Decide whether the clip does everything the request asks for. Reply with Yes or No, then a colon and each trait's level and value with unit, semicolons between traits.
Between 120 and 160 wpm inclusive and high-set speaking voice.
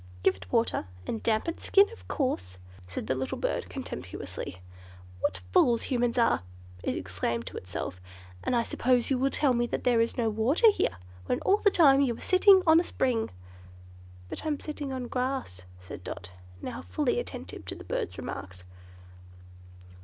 No: average, 175 wpm; high, 240 Hz